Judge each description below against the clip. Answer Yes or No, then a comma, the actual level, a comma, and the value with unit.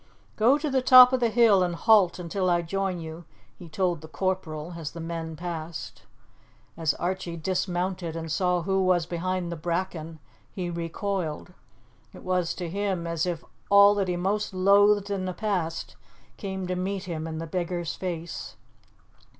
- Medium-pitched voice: Yes, medium, 180 Hz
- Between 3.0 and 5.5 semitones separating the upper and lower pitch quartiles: No, narrow, 2.6 semitones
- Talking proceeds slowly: No, average, 170 wpm